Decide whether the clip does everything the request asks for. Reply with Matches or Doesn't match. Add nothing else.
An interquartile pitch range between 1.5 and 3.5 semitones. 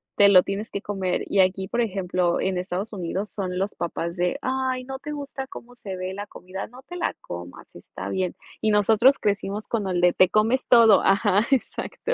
Doesn't match